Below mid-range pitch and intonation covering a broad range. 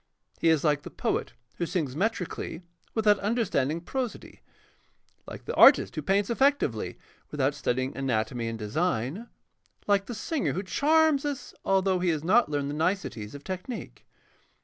No: medium, 180 Hz; wide, 7.6 semitones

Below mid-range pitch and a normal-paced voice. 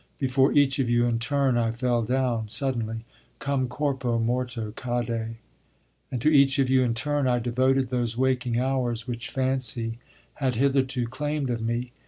Yes: low, 125 Hz; average, 165 wpm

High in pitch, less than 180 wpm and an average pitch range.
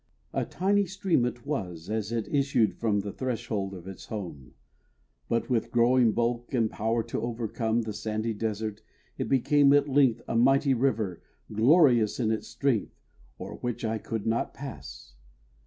No: low, 115 Hz; average, 160 wpm; average, 3.2 semitones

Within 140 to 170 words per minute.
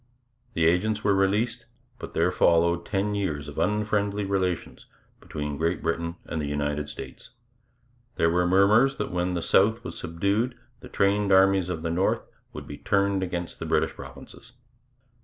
Yes: average, 160 wpm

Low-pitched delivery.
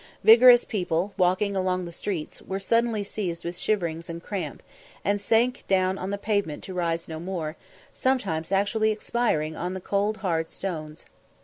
No: high, 190 Hz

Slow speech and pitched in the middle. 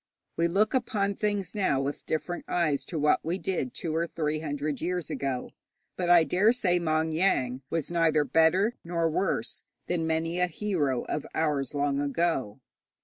No: average, 170 wpm; medium, 165 Hz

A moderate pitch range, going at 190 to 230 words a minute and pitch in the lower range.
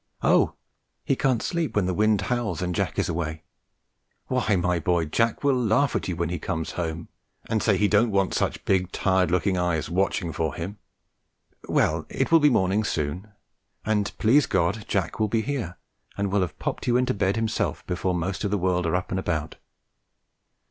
Yes: average, 3.9 semitones; average, 195 wpm; very low, 95 Hz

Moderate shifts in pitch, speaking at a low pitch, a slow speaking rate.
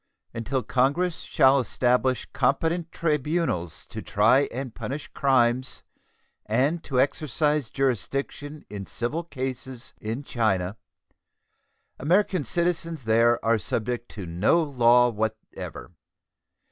Yes: average, 4.3 semitones; low, 130 Hz; slow, 105 wpm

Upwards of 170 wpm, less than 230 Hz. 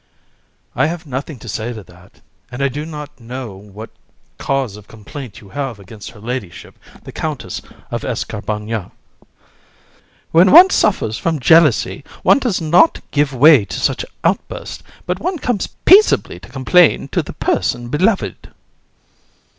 No: average, 155 wpm; low, 135 Hz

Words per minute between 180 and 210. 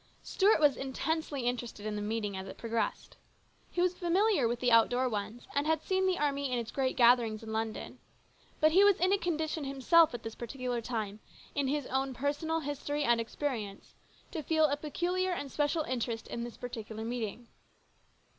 Yes: average, 185 wpm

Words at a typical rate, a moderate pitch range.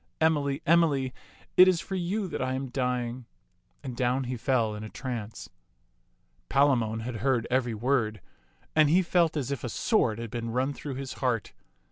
Yes: average, 180 wpm; average, 3.6 semitones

